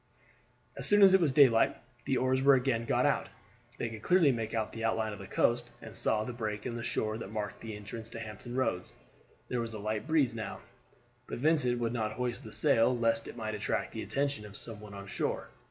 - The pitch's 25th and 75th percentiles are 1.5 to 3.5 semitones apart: Yes, average, 2.8 semitones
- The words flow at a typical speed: No, fast, 230 wpm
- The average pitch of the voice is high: No, low, 115 Hz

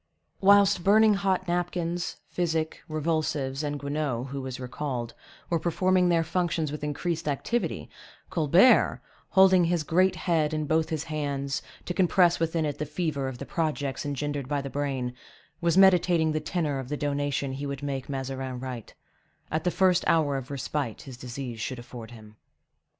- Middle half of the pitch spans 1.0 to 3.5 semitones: No, average, 4.1 semitones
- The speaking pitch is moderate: Yes, medium, 150 Hz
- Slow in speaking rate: No, average, 165 wpm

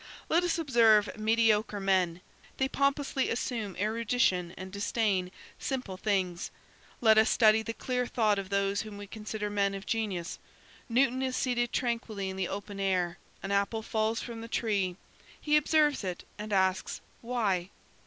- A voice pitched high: Yes, high, 215 Hz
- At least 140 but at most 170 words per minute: Yes, average, 155 wpm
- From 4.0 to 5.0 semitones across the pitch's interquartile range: No, average, 3.3 semitones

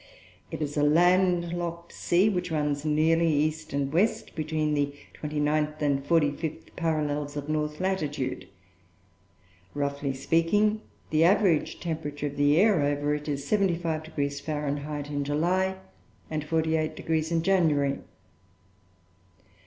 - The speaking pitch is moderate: Yes, medium, 155 Hz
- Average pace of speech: No, slow, 125 wpm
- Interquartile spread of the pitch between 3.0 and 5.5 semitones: No, narrow, 2.5 semitones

